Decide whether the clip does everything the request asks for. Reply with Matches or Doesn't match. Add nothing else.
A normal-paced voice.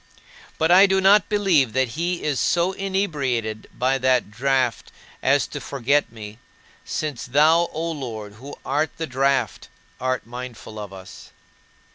Matches